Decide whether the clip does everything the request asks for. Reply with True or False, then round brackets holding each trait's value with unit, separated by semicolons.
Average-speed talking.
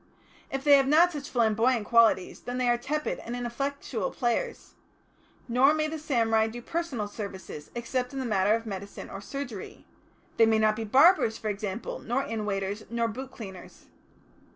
True (175 wpm)